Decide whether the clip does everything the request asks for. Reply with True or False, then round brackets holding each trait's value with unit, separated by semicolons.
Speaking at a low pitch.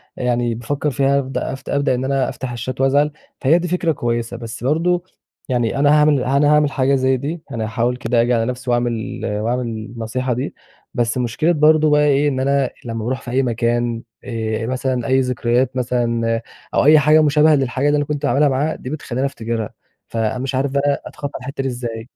True (130 Hz)